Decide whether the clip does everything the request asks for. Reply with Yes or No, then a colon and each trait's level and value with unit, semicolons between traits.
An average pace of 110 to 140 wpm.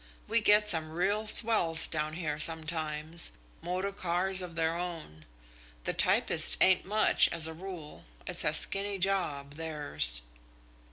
Yes: slow, 135 wpm